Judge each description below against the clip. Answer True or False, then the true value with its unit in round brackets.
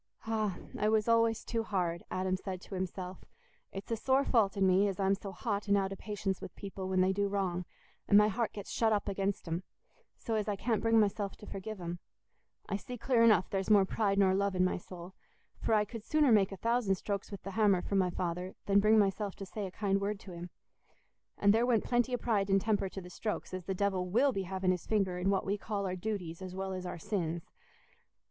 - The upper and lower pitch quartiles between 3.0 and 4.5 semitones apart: False (2.4 semitones)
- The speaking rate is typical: False (240 wpm)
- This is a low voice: False (195 Hz)